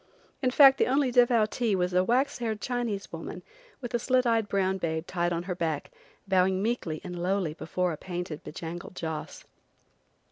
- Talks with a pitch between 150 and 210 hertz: Yes, high, 190 Hz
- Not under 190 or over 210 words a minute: No, average, 180 wpm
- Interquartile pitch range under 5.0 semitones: No, wide, 5.5 semitones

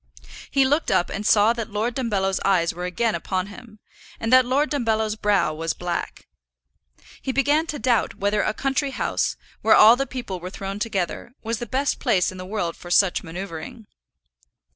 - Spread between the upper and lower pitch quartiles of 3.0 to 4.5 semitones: No, average, 5.0 semitones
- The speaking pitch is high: Yes, high, 215 Hz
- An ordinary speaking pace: Yes, average, 185 wpm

